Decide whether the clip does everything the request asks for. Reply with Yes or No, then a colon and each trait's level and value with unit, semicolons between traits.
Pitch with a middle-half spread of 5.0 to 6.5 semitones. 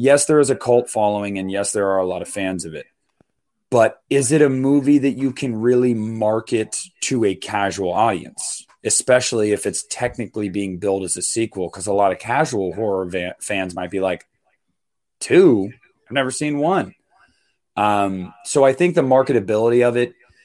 Yes: average, 5.3 semitones